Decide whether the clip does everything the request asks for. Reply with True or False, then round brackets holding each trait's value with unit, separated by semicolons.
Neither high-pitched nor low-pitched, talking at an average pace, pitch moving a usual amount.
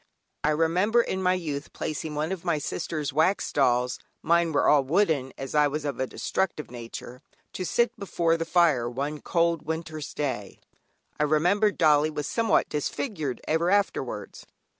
True (155 Hz; 160 wpm; 3.4 semitones)